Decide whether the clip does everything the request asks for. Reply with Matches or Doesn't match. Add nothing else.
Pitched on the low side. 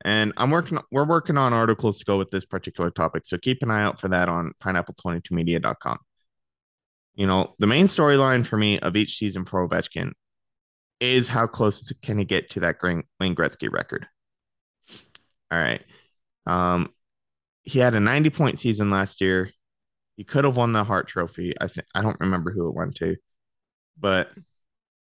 Matches